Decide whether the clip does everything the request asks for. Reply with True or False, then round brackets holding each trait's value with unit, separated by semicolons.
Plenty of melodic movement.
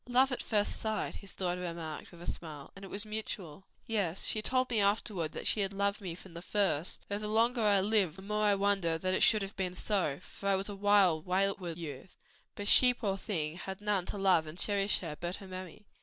False (2.9 semitones)